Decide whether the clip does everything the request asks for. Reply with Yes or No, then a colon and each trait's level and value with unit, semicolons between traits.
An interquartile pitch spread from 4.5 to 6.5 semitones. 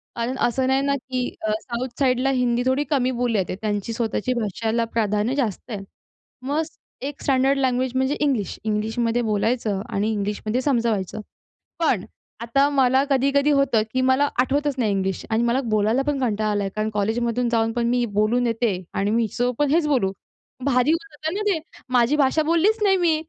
No: average, 3.8 semitones